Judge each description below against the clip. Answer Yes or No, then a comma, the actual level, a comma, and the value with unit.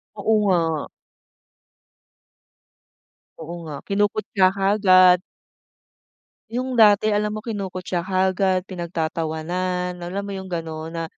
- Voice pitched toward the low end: No, medium, 185 Hz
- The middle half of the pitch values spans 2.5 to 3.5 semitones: Yes, average, 2.8 semitones